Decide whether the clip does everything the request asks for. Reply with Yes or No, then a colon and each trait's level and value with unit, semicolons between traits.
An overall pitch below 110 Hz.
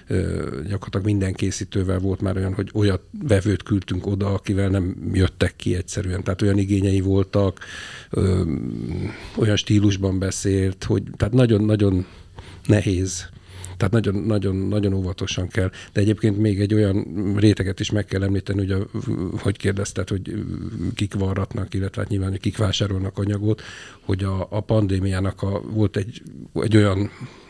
Yes: low, 100 Hz